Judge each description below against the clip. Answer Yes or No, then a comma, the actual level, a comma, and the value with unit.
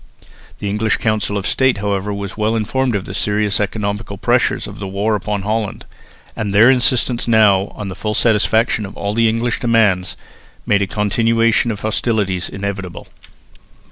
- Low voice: Yes, low, 105 Hz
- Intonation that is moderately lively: No, narrow, 2.1 semitones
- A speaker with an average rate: Yes, average, 165 wpm